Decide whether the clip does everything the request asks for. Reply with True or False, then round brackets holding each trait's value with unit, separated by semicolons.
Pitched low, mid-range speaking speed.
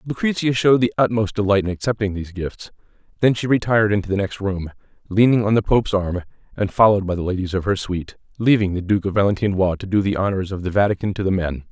False (100 Hz; 225 wpm)